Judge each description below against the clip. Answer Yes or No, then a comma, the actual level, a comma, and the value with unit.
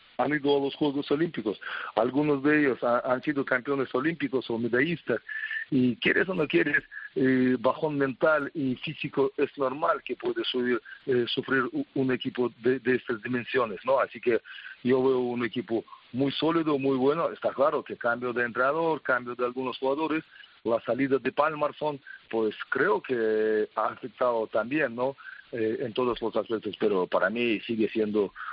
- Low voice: Yes, low, 130 Hz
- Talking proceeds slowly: No, average, 170 wpm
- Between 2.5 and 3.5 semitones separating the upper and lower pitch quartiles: Yes, average, 3.2 semitones